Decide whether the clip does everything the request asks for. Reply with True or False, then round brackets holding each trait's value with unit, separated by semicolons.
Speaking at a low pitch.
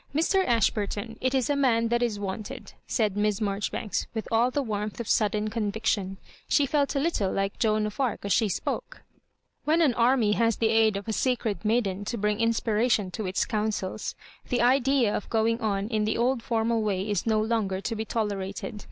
False (220 Hz)